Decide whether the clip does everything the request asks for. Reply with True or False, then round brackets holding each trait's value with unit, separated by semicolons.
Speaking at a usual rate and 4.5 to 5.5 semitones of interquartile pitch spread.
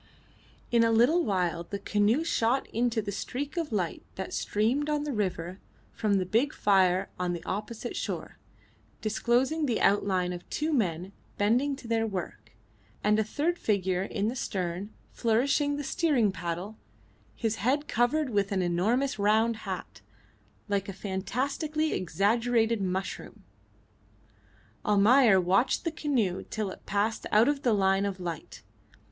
True (150 wpm; 4.8 semitones)